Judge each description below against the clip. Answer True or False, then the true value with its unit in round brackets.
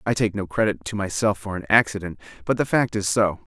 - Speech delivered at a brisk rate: True (235 wpm)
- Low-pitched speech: True (100 Hz)